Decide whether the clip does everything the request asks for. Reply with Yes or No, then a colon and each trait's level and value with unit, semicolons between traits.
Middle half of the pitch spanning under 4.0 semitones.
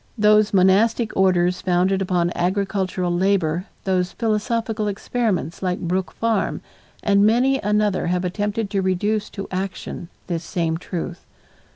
Yes: average, 2.7 semitones